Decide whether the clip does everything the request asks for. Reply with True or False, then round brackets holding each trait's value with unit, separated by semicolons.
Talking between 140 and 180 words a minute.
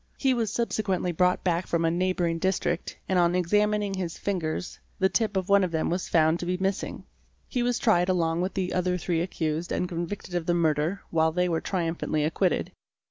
False (205 wpm)